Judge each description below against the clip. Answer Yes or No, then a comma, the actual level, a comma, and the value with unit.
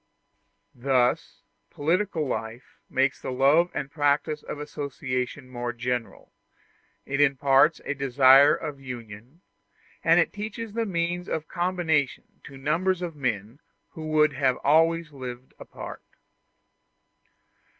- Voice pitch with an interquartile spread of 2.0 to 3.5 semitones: No, average, 4.1 semitones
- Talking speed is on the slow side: Yes, slow, 115 wpm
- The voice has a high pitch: No, medium, 140 Hz